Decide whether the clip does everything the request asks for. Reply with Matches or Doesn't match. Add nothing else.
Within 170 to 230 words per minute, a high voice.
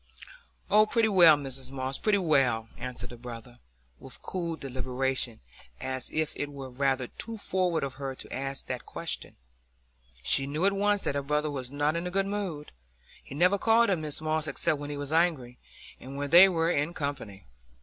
Doesn't match